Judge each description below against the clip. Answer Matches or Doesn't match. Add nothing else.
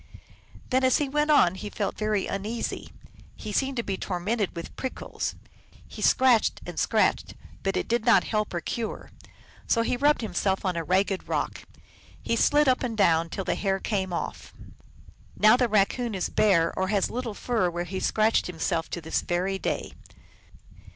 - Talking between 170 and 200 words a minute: Matches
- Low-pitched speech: Doesn't match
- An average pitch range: Matches